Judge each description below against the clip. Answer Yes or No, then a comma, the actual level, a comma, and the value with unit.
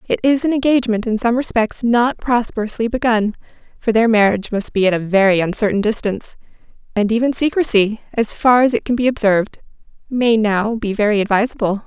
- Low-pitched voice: No, high, 225 Hz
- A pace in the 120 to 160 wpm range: No, average, 175 wpm